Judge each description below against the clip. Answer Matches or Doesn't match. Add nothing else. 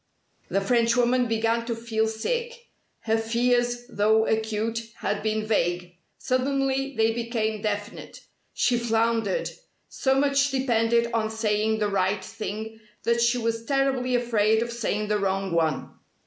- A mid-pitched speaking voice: Doesn't match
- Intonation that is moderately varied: Doesn't match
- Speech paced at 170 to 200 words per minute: Doesn't match